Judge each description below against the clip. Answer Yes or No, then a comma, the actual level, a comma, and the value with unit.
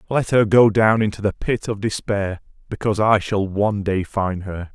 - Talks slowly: No, average, 200 wpm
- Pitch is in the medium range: No, low, 105 Hz